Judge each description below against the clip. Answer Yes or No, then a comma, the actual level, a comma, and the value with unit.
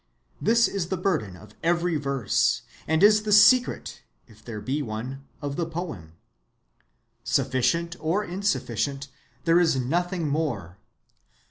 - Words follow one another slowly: Yes, slow, 130 wpm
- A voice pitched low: No, medium, 155 Hz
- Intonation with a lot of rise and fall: Yes, wide, 5.8 semitones